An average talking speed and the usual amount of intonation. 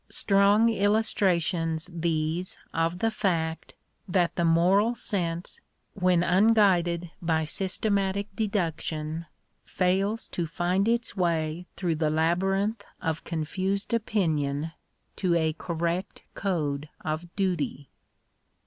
No: slow, 105 wpm; average, 3.4 semitones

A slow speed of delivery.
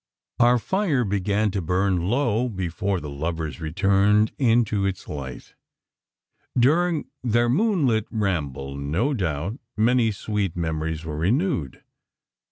Yes: slow, 115 wpm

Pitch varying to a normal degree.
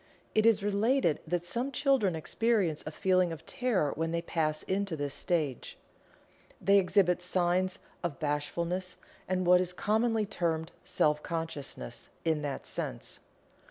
Yes: average, 3.9 semitones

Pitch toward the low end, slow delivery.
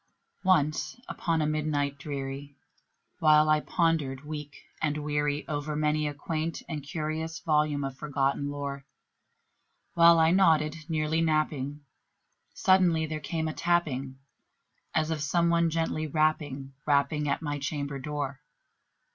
No: medium, 150 Hz; slow, 130 wpm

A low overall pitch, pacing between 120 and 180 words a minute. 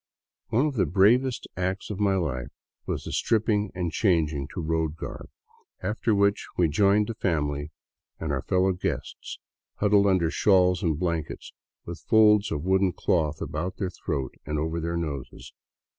Yes: very low, 90 Hz; average, 160 wpm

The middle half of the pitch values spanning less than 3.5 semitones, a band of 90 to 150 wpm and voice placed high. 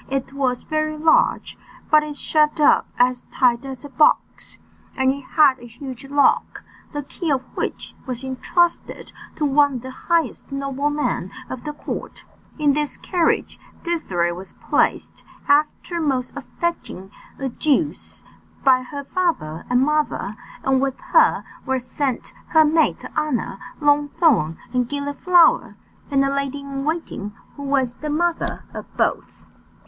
Yes: average, 2.9 semitones; average, 145 wpm; very high, 280 Hz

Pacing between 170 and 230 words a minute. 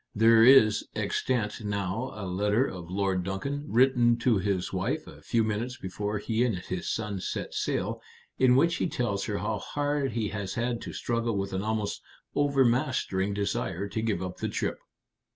Yes: average, 175 wpm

